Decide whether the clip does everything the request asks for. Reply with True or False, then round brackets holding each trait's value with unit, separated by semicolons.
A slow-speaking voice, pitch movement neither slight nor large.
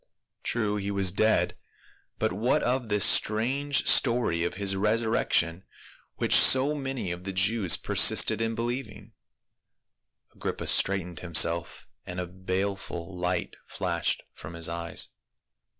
True (125 wpm; 4.4 semitones)